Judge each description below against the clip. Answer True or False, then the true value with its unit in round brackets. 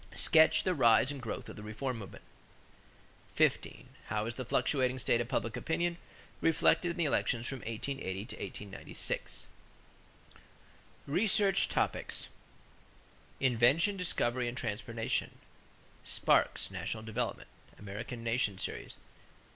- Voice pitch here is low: True (120 Hz)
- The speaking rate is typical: False (120 wpm)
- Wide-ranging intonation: False (4.5 semitones)